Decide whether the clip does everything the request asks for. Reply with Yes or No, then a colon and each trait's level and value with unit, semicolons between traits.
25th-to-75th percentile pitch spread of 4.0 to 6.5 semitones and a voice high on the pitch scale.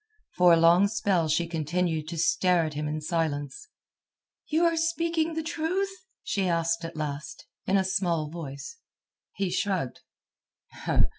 No: average, 4.5 semitones; medium, 175 Hz